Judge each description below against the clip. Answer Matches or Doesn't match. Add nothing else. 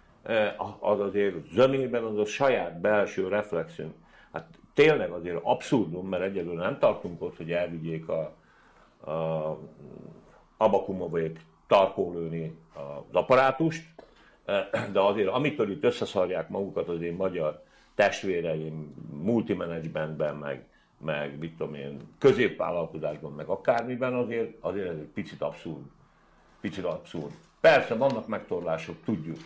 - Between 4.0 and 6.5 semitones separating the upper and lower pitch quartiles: Matches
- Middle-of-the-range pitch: Doesn't match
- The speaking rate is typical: Matches